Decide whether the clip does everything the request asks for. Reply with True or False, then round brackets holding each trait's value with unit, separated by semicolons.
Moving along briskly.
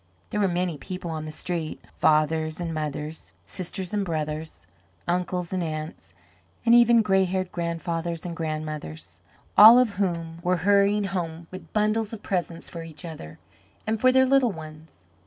False (160 wpm)